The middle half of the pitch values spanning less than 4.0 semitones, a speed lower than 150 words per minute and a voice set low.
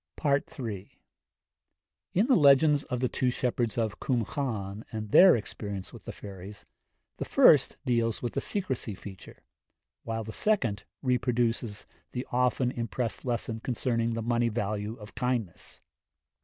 Yes: average, 2.9 semitones; average, 140 wpm; low, 115 Hz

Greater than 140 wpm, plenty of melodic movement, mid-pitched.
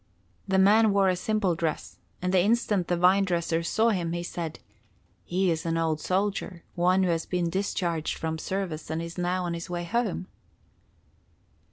No: average, 180 wpm; narrow, 2.4 semitones; medium, 180 Hz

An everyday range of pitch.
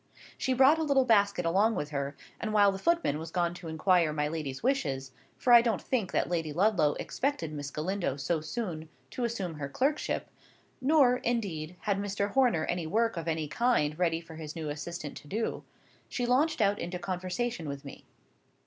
No: wide, 7.0 semitones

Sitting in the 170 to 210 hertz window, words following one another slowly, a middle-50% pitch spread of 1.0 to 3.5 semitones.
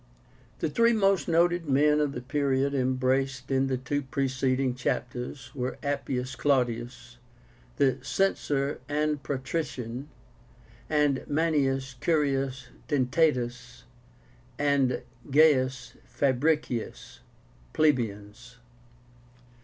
No: low, 135 Hz; slow, 90 wpm; narrow, 2.6 semitones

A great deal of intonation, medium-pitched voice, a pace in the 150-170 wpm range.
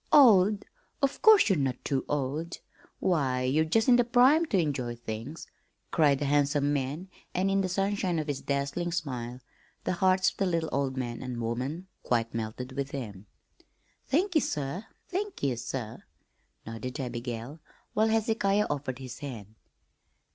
Yes: wide, 7.1 semitones; medium, 145 Hz; average, 160 wpm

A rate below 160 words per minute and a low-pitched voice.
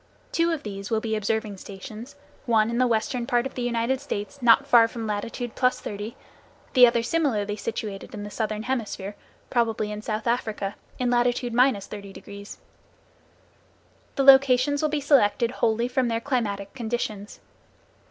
No: average, 150 wpm; high, 230 Hz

